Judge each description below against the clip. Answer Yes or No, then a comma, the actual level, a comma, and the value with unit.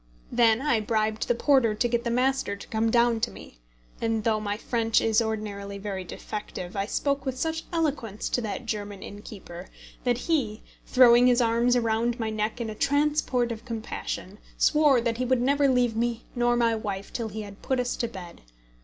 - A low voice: No, high, 230 Hz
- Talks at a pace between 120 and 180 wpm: No, average, 195 wpm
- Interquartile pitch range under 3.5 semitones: Yes, narrow, 2.6 semitones